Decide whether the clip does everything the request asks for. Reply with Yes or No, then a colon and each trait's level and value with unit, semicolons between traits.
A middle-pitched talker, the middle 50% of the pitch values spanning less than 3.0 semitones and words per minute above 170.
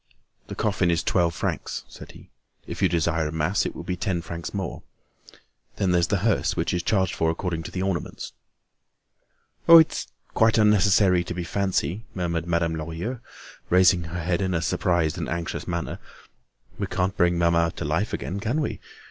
No: very low, 90 Hz; narrow, 2.6 semitones; average, 180 wpm